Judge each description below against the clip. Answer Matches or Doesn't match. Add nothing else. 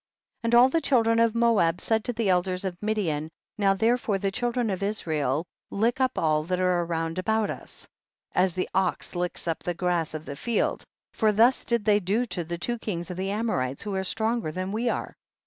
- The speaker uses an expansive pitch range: Doesn't match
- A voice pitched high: Matches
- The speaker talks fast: Matches